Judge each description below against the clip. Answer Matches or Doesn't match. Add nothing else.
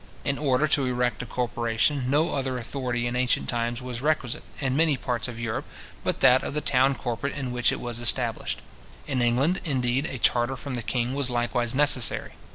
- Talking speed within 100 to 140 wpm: Doesn't match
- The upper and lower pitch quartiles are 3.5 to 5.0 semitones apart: Doesn't match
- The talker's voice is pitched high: Doesn't match